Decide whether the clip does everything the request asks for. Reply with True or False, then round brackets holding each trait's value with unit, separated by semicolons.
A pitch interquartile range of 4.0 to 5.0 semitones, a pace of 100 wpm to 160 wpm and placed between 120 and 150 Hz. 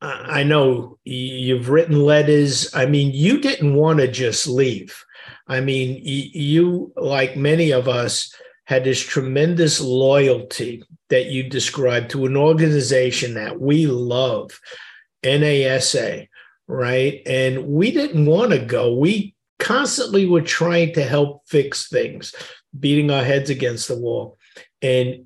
False (3.2 semitones; 135 wpm; 140 Hz)